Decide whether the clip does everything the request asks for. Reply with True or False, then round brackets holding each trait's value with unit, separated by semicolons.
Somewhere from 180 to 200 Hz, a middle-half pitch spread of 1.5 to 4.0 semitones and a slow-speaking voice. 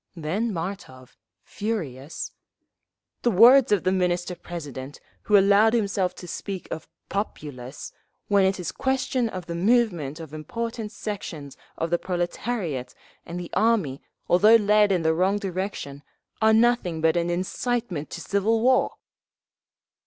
False (185 Hz; 5.0 semitones; 130 wpm)